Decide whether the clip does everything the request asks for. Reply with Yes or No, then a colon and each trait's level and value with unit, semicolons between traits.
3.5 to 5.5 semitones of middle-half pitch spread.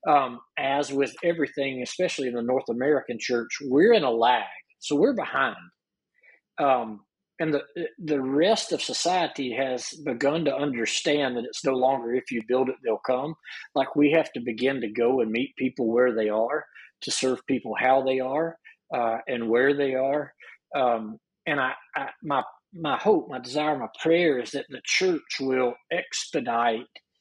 No: average, 3.1 semitones